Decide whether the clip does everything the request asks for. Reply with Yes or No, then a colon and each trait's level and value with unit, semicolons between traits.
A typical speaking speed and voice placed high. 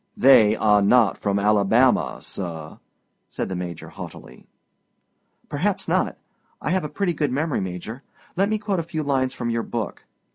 No: average, 160 wpm; low, 120 Hz